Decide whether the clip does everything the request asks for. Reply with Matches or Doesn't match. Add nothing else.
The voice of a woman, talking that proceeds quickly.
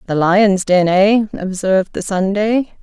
Doesn't match